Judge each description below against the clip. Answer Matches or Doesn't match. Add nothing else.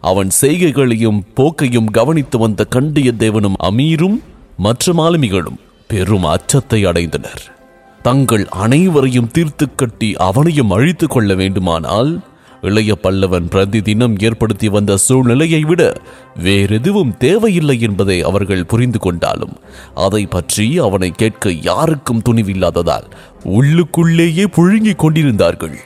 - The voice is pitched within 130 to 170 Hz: Doesn't match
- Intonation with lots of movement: Matches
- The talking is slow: Matches